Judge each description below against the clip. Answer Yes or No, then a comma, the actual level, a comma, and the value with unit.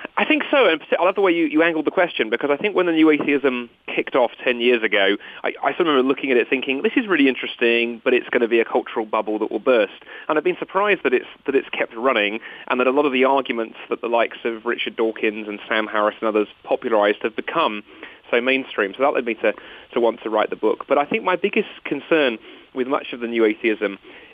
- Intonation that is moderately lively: No, wide, 6.5 semitones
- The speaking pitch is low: Yes, low, 130 Hz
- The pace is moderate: No, fast, 255 wpm